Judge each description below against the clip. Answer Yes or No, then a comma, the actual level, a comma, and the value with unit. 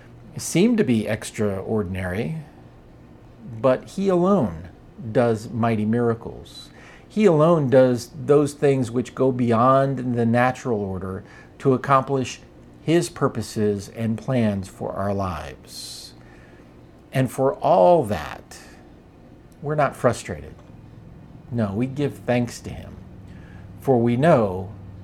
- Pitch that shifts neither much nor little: No, wide, 5.8 semitones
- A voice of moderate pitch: No, low, 115 Hz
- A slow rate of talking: Yes, slow, 110 wpm